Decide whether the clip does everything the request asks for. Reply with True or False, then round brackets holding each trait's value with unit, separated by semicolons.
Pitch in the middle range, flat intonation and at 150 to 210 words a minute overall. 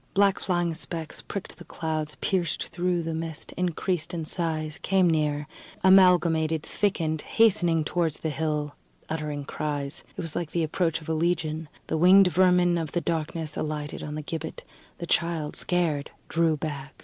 True (165 Hz; 2.3 semitones; 160 wpm)